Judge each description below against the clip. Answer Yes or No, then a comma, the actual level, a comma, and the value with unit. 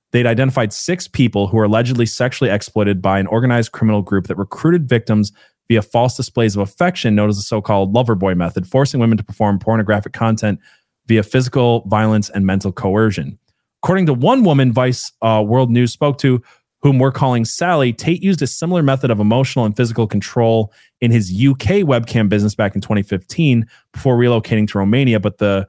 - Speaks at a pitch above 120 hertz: No, low, 115 Hz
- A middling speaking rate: Yes, average, 185 wpm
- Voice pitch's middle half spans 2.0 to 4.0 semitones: Yes, average, 3.6 semitones